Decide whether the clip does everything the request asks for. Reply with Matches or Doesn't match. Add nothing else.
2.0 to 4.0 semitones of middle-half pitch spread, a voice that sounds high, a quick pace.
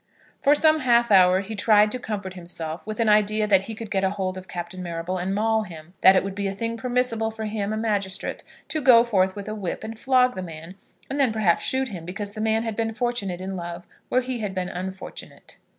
Matches